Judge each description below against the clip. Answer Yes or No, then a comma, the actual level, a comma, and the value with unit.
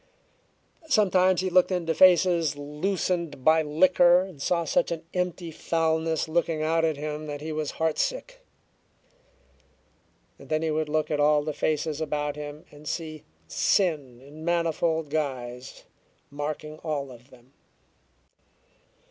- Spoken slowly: Yes, slow, 130 wpm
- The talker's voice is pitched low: No, medium, 155 Hz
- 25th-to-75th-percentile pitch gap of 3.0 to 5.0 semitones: No, narrow, 2.5 semitones